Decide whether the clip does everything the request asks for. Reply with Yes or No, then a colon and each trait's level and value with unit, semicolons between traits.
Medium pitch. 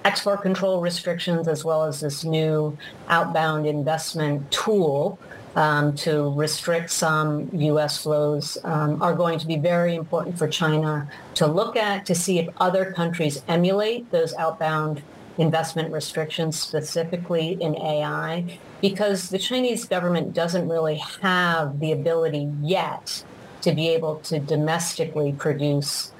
Yes: medium, 160 Hz